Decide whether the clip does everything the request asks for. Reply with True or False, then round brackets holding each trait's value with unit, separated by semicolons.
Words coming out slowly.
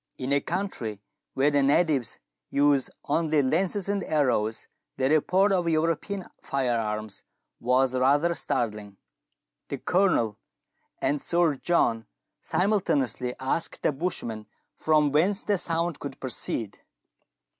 True (120 wpm)